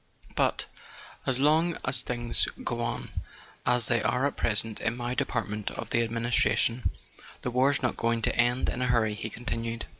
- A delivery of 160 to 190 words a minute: Yes, average, 175 wpm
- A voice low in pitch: Yes, low, 120 Hz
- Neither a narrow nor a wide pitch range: No, narrow, 1.5 semitones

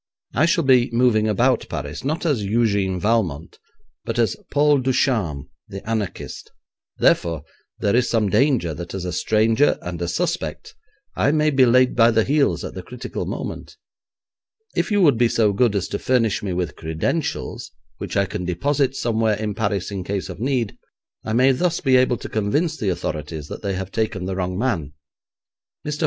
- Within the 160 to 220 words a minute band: Yes, average, 180 wpm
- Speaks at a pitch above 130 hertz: No, low, 110 Hz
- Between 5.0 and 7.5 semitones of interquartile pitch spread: Yes, wide, 5.4 semitones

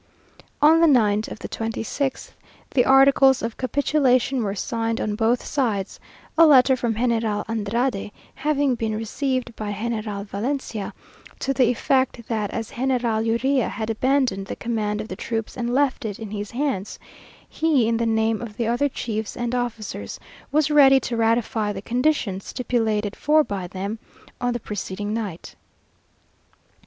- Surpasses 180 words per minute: No, average, 160 wpm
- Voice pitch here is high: Yes, high, 230 Hz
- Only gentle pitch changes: No, average, 3.5 semitones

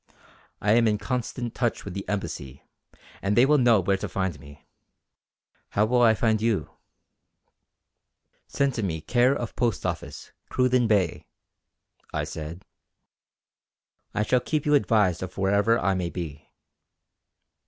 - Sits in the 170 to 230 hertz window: No, low, 105 Hz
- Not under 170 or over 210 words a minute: No, average, 145 wpm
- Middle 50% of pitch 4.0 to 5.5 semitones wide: Yes, average, 4.7 semitones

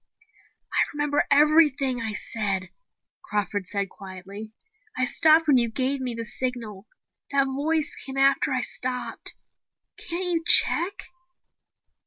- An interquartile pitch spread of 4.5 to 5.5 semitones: Yes, average, 5.2 semitones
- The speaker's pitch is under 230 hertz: No, very high, 255 Hz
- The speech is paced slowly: Yes, slow, 125 wpm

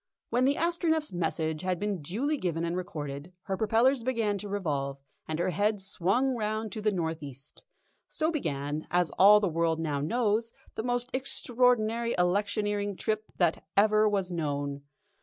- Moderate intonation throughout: No, wide, 5.7 semitones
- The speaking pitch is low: No, high, 205 Hz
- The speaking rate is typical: Yes, average, 160 wpm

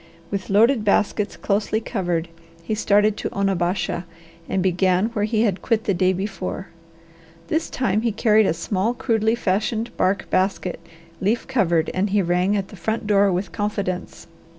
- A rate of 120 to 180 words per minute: Yes, average, 160 wpm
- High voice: Yes, high, 200 Hz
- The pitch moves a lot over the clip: No, average, 2.8 semitones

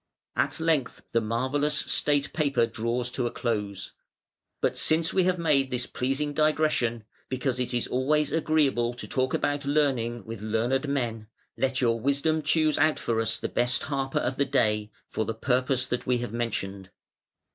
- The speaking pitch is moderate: No, low, 130 Hz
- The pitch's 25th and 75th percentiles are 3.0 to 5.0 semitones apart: Yes, average, 3.8 semitones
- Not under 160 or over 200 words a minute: Yes, average, 170 wpm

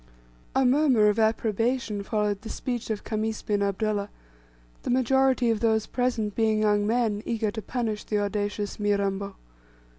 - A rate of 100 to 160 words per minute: Yes, average, 150 wpm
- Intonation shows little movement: Yes, narrow, 2.3 semitones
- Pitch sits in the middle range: No, high, 215 Hz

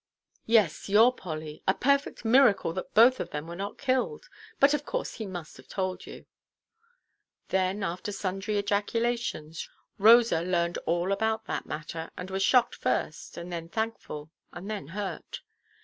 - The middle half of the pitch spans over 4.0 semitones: Yes, average, 4.9 semitones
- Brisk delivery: No, average, 155 wpm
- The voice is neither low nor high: No, high, 195 Hz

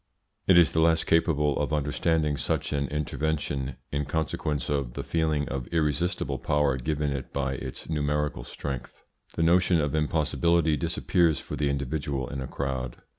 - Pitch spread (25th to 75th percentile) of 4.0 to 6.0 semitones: No, narrow, 2.5 semitones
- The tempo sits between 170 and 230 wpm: No, average, 160 wpm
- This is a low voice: Yes, very low, 75 Hz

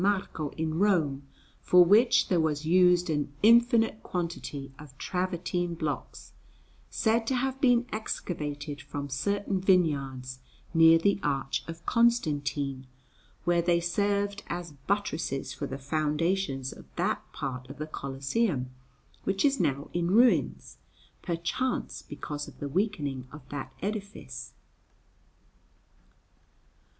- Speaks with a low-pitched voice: No, medium, 170 Hz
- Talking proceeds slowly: Yes, slow, 120 wpm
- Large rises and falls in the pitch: Yes, wide, 5.9 semitones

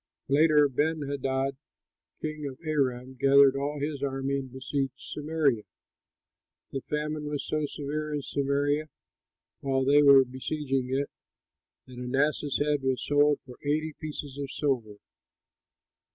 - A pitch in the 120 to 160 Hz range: Yes, medium, 140 Hz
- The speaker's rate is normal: No, slow, 130 wpm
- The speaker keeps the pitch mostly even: Yes, narrow, 1.9 semitones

